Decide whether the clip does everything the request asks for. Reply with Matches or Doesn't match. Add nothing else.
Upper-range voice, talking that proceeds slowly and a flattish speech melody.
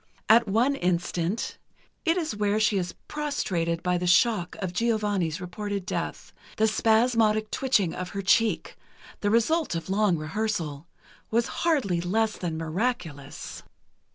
Doesn't match